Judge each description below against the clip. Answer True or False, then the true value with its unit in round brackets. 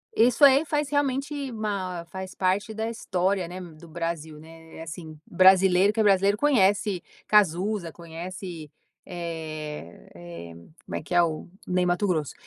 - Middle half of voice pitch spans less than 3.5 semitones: False (4.2 semitones)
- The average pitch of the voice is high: False (180 Hz)